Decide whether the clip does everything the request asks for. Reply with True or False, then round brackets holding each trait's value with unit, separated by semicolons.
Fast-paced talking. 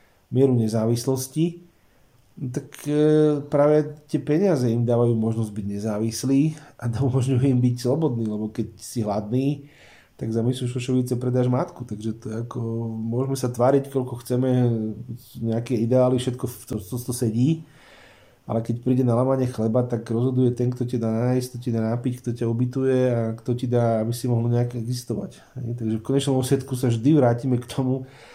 True (175 wpm)